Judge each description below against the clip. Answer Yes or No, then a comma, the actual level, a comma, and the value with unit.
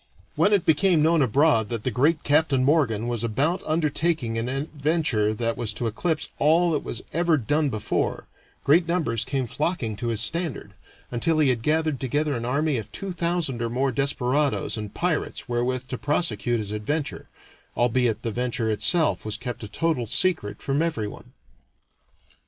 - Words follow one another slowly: No, average, 170 wpm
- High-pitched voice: No, low, 135 Hz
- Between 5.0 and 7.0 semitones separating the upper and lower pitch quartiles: Yes, wide, 5.4 semitones